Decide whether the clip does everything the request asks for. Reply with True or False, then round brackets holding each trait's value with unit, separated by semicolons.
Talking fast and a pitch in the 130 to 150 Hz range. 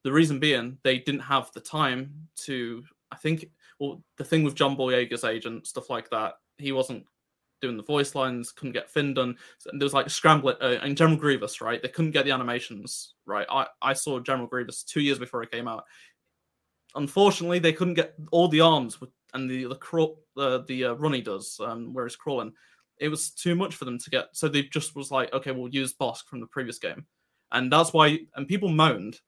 True (220 wpm; 135 Hz)